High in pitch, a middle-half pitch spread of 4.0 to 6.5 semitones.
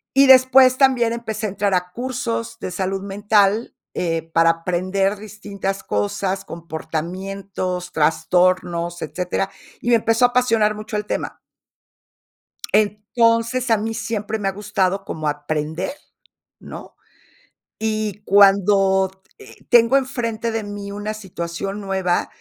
No: high, 200 Hz; average, 3.3 semitones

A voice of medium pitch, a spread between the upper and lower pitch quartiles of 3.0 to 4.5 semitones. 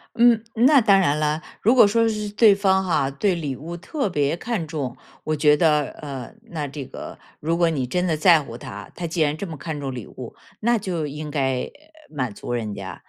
No: medium, 160 Hz; wide, 5.6 semitones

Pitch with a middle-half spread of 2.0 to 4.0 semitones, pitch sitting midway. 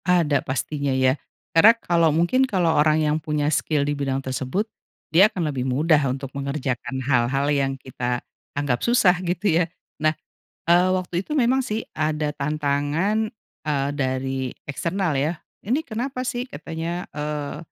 No: average, 4.5 semitones; medium, 155 Hz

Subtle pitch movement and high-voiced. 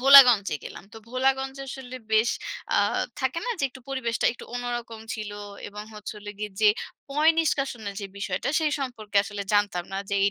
No: average, 4.3 semitones; high, 240 Hz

